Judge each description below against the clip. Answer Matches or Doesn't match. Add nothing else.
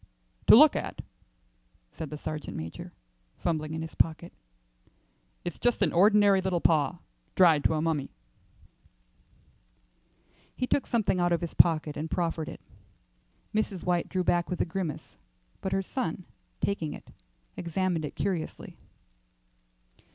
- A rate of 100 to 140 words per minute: Matches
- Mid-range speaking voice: Matches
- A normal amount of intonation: Matches